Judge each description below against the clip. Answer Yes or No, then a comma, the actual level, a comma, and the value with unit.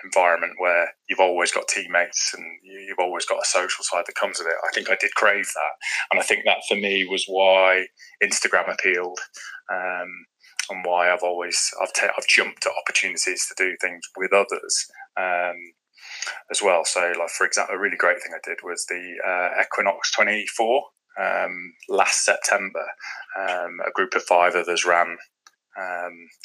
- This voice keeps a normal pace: Yes, average, 180 wpm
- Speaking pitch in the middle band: No, very low, 90 Hz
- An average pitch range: No, narrow, 1.4 semitones